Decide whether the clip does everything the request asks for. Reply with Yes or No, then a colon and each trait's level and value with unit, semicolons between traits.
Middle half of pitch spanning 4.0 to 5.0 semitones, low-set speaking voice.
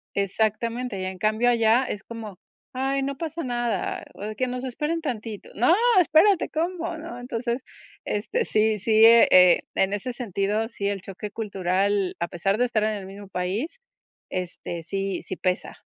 No: average, 4.3 semitones; high, 220 Hz